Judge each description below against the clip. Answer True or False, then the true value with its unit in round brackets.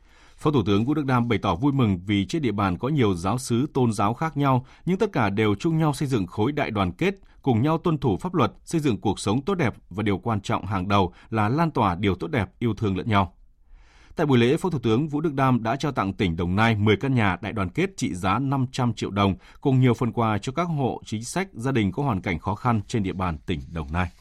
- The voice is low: True (115 Hz)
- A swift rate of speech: True (275 wpm)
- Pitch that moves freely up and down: True (5.7 semitones)